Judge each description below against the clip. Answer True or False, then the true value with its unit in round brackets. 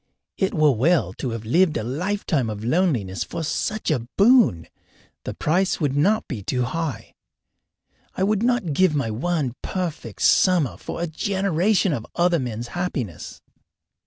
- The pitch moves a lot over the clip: True (7.5 semitones)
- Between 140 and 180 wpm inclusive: True (155 wpm)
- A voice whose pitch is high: False (155 Hz)